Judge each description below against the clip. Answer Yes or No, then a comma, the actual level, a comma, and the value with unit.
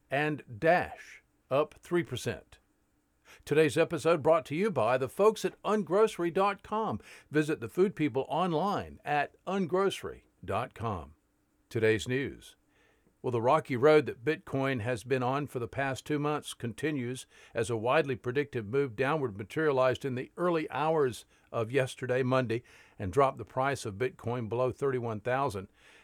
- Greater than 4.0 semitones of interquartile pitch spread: Yes, average, 4.5 semitones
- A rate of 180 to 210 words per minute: No, average, 140 wpm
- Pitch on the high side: No, low, 135 Hz